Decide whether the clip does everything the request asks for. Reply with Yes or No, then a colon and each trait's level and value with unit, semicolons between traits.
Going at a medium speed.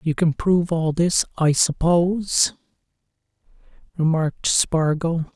No: slow, 100 wpm